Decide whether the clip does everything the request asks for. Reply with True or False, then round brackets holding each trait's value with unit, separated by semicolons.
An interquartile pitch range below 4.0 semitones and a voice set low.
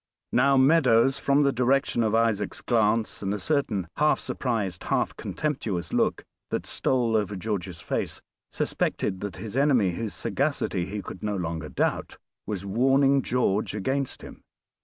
False (5.2 semitones; 115 Hz)